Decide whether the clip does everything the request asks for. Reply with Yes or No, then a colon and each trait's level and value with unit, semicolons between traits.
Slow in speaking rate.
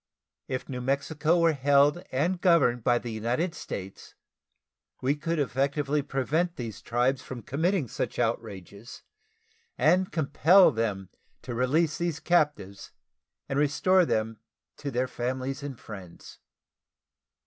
Yes: slow, 125 wpm